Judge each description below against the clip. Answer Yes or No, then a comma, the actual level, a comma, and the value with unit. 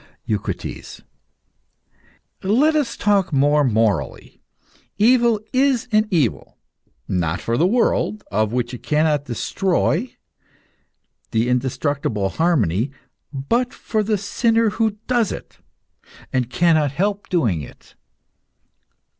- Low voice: No, medium, 160 Hz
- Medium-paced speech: No, slow, 105 wpm